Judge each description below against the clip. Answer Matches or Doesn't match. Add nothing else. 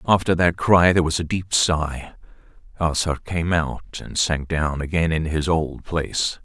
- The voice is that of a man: Matches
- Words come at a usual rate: Matches